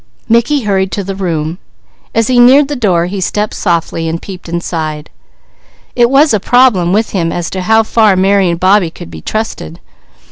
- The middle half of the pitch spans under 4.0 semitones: No, average, 4.7 semitones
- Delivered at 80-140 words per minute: No, average, 185 wpm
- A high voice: Yes, high, 195 Hz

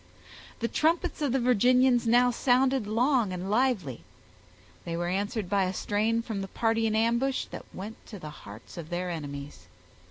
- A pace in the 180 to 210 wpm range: No, average, 170 wpm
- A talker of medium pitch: No, high, 220 Hz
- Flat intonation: No, wide, 5.4 semitones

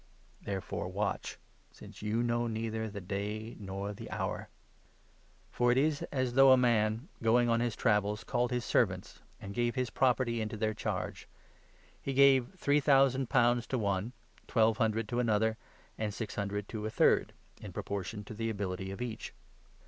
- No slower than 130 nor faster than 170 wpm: No, average, 185 wpm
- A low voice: Yes, low, 115 Hz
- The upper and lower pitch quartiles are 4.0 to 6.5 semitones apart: No, average, 2.8 semitones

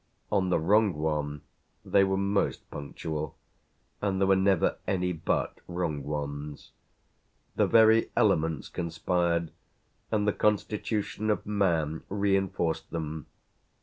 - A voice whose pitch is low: Yes, very low, 90 Hz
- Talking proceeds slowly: Yes, slow, 115 wpm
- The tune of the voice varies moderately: Yes, average, 4.2 semitones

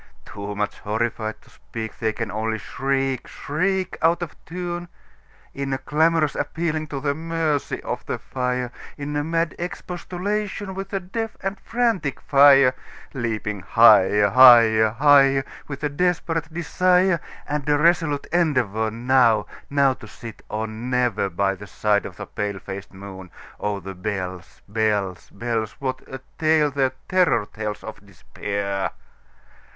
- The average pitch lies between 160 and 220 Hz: No, low, 130 Hz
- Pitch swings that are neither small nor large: No, wide, 7.0 semitones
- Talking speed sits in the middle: No, slow, 120 wpm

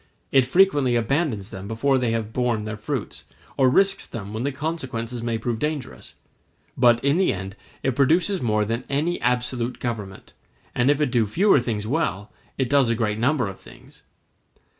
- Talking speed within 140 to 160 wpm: No, average, 180 wpm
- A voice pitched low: Yes, low, 125 Hz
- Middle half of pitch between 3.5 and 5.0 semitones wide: Yes, average, 4.1 semitones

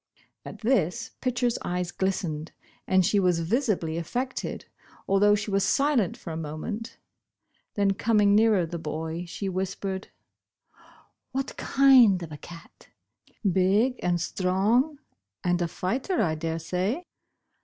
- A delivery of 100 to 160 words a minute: Yes, average, 145 wpm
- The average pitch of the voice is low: No, high, 190 Hz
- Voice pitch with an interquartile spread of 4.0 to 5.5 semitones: Yes, average, 4.7 semitones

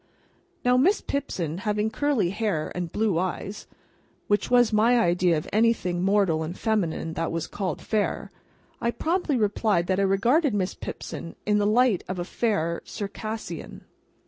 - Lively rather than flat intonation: No, average, 4.5 semitones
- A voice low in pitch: No, high, 205 Hz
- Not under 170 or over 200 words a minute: No, average, 155 wpm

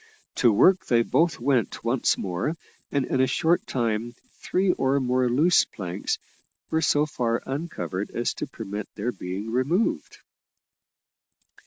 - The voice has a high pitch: No, low, 125 Hz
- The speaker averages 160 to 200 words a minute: No, average, 140 wpm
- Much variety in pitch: No, average, 4.8 semitones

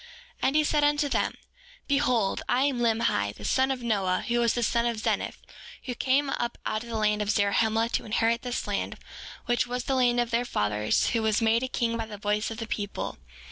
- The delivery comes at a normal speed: No, fast, 225 wpm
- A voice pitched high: Yes, high, 235 Hz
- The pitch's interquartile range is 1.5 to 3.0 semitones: Yes, narrow, 2.5 semitones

